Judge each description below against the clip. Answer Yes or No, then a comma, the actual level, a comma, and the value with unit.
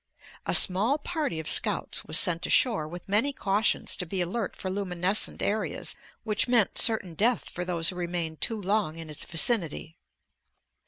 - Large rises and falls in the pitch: No, average, 4.4 semitones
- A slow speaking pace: No, average, 165 wpm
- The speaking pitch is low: No, medium, 185 Hz